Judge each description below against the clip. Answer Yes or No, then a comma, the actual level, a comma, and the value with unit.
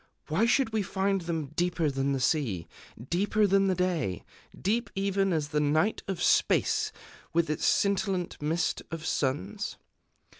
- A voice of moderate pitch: Yes, medium, 175 Hz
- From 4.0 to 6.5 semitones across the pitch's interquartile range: Yes, average, 4.7 semitones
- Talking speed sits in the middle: Yes, average, 150 wpm